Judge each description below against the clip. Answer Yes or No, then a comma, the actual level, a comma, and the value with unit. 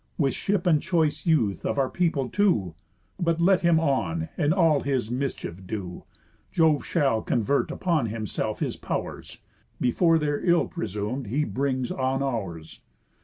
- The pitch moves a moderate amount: No, wide, 5.7 semitones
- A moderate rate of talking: Yes, average, 150 wpm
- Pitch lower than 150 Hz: Yes, medium, 140 Hz